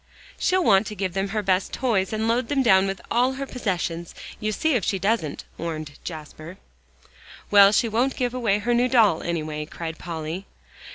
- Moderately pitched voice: No, high, 200 Hz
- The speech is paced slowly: No, average, 185 wpm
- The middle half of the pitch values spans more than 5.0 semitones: Yes, wide, 5.5 semitones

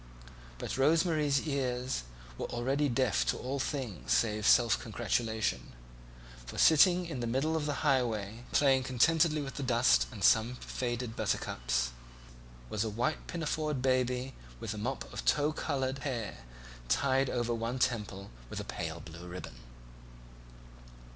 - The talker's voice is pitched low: Yes, low, 125 Hz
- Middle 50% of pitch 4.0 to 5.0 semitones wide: Yes, average, 4.3 semitones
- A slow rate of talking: No, average, 145 wpm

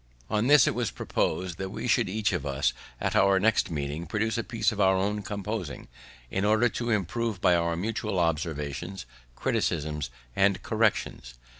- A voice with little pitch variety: No, average, 4.3 semitones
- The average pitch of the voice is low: Yes, very low, 95 Hz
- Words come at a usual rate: Yes, average, 170 wpm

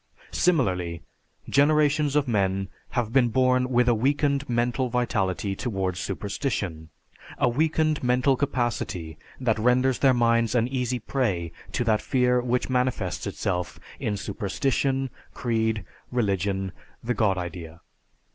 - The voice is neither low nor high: No, low, 120 Hz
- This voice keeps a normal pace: No, slow, 125 wpm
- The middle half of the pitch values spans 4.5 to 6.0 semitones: Yes, average, 5.0 semitones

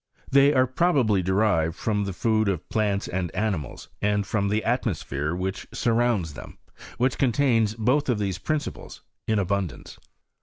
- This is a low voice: Yes, low, 105 Hz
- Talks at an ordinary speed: Yes, average, 155 wpm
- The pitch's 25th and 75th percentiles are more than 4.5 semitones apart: No, average, 4.2 semitones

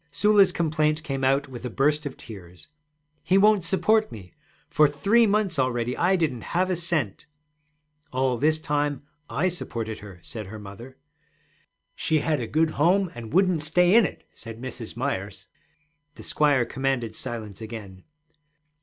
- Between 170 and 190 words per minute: No, average, 155 wpm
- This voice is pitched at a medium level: Yes, medium, 145 Hz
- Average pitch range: No, wide, 6.6 semitones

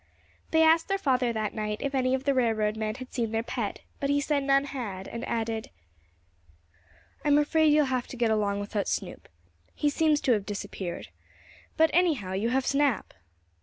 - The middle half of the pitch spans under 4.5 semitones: No, average, 4.8 semitones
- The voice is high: Yes, very high, 255 Hz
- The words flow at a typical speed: Yes, average, 185 wpm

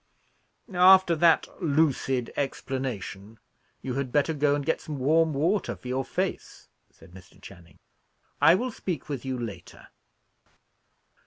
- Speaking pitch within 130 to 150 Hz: Yes, medium, 140 Hz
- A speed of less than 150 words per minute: Yes, slow, 135 wpm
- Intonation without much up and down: No, average, 4.4 semitones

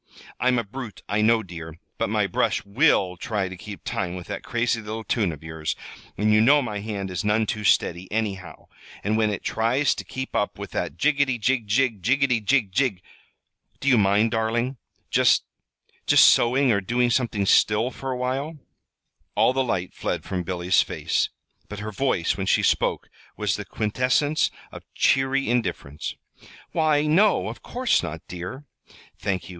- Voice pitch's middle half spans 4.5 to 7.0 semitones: Yes, average, 4.8 semitones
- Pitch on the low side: Yes, low, 110 Hz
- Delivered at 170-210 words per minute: Yes, average, 175 wpm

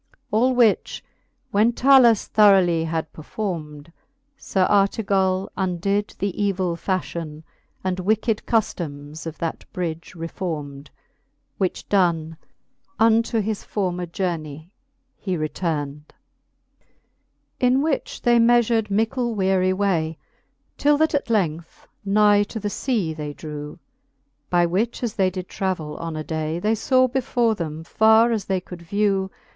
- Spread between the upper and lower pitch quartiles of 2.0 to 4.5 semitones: No, average, 5.0 semitones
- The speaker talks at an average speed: No, slow, 130 wpm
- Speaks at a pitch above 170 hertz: Yes, high, 190 Hz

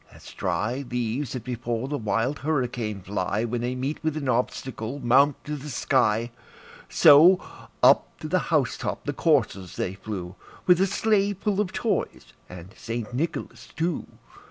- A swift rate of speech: No, average, 160 wpm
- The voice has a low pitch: Yes, low, 125 Hz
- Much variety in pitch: No, average, 5.0 semitones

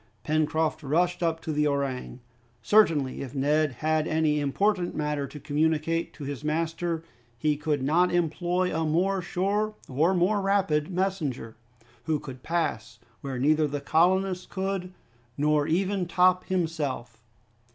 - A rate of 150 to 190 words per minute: No, average, 140 wpm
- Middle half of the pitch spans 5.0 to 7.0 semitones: No, average, 3.5 semitones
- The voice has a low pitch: No, medium, 160 Hz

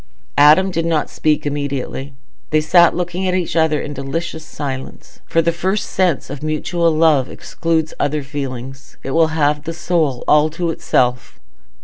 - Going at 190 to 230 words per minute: No, average, 155 wpm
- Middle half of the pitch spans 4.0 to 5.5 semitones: No, average, 2.8 semitones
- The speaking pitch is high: No, medium, 155 Hz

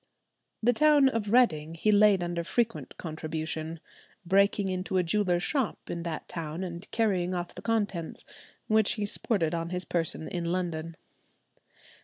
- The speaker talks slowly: No, average, 150 wpm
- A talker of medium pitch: Yes, medium, 180 Hz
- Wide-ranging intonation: No, average, 4.0 semitones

